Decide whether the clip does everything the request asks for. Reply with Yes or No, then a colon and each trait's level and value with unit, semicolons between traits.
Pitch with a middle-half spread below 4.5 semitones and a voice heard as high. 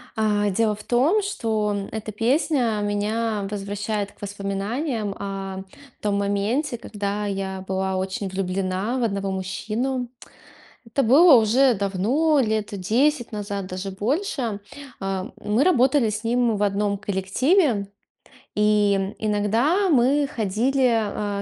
Yes: average, 3.6 semitones; high, 210 Hz